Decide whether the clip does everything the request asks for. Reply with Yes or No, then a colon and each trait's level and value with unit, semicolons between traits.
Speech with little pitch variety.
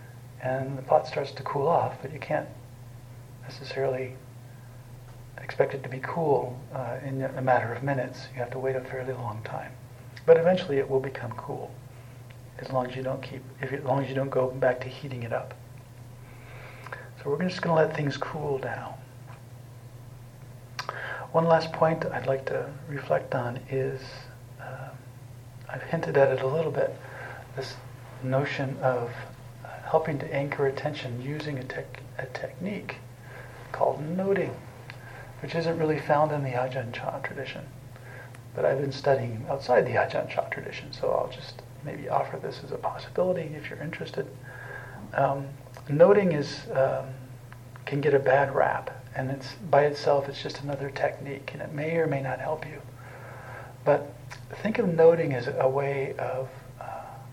Yes: narrow, 1.9 semitones